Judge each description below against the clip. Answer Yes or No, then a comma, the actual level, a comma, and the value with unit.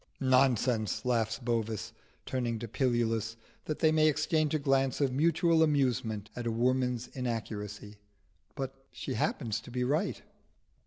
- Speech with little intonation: No, average, 3.3 semitones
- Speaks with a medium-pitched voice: No, low, 125 Hz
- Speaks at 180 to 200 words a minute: No, average, 140 wpm